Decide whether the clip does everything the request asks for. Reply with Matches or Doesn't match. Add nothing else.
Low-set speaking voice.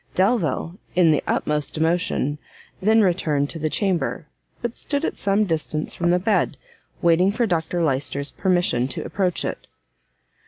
Doesn't match